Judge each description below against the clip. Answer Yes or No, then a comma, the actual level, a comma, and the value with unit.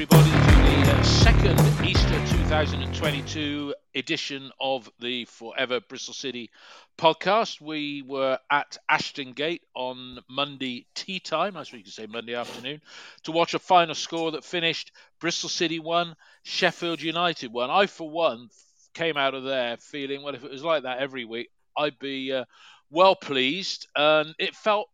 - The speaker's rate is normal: Yes, average, 160 wpm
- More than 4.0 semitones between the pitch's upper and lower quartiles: Yes, average, 4.4 semitones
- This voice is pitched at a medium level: Yes, medium, 145 Hz